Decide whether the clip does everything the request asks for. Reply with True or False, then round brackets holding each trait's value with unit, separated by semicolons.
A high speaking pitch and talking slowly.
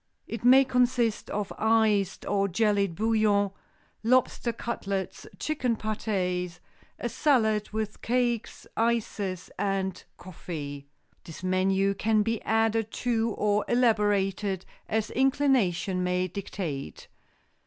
True (210 Hz; 105 wpm)